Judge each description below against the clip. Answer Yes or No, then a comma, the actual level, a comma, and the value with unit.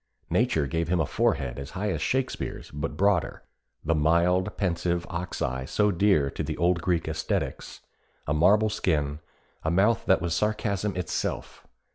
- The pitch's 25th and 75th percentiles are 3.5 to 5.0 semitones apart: Yes, average, 4.2 semitones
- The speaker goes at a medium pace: Yes, average, 160 wpm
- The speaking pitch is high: No, very low, 85 Hz